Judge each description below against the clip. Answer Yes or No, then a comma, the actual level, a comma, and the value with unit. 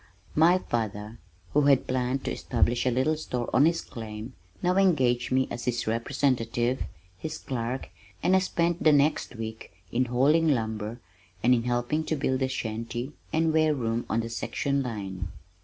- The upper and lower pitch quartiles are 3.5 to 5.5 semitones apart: Yes, average, 4.3 semitones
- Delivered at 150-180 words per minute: Yes, average, 170 wpm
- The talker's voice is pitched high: No, low, 125 Hz